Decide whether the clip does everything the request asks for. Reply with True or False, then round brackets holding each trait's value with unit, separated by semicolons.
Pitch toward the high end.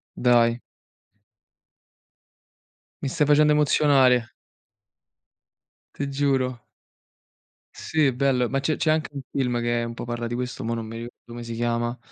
False (125 Hz)